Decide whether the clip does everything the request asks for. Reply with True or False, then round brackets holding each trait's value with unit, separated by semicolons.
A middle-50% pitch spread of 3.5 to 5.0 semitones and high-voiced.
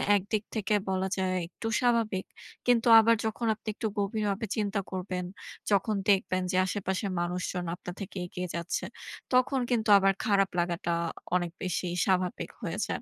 False (3.0 semitones; 195 Hz)